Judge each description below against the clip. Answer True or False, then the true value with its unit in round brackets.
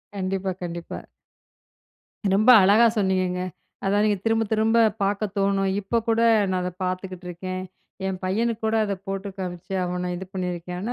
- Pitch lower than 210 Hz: True (190 Hz)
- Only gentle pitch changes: True (2.2 semitones)